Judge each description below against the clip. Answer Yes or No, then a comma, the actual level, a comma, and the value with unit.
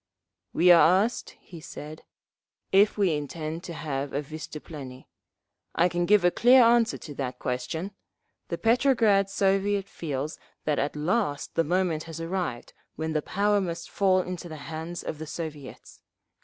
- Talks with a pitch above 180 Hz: No, medium, 170 Hz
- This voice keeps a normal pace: Yes, average, 155 wpm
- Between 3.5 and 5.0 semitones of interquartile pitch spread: Yes, average, 4.2 semitones